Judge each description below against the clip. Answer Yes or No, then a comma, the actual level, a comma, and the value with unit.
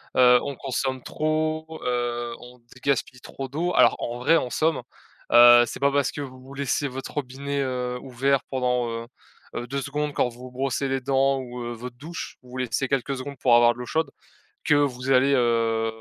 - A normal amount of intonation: No, narrow, 2.2 semitones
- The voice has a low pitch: Yes, low, 130 Hz